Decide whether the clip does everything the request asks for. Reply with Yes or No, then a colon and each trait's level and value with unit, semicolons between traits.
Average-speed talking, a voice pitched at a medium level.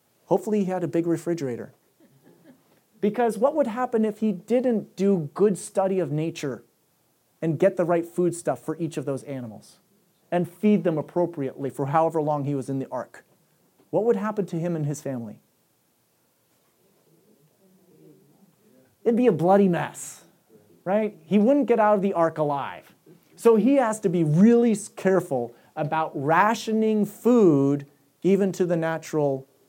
Yes: average, 155 wpm; medium, 175 Hz